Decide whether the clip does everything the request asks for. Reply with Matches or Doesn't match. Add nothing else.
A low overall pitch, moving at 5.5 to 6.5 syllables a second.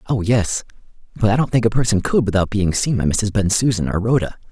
Matches